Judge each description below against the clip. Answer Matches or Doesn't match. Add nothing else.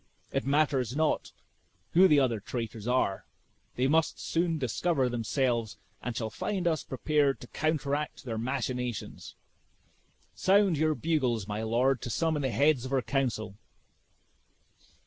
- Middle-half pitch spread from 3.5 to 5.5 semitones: Matches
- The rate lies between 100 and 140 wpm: Matches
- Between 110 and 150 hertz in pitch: Matches